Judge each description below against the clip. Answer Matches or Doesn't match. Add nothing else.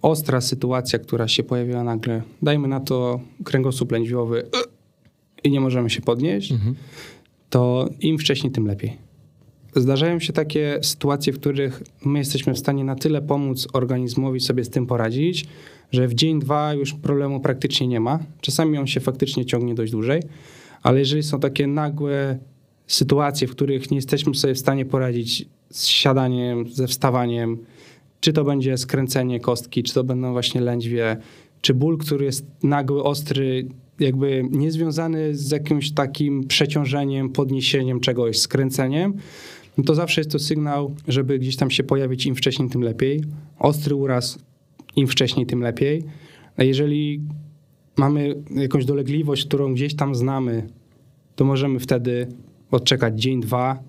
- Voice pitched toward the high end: Doesn't match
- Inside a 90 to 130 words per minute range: Doesn't match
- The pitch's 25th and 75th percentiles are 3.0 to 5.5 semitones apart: Doesn't match